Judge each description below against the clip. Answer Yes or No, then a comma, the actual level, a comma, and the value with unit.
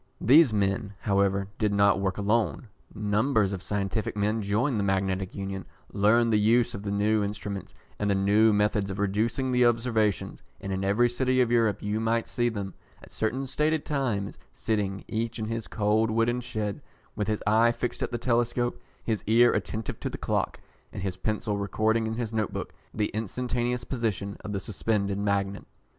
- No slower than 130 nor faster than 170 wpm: No, average, 180 wpm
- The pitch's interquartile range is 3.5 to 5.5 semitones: No, narrow, 2.6 semitones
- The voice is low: Yes, low, 105 Hz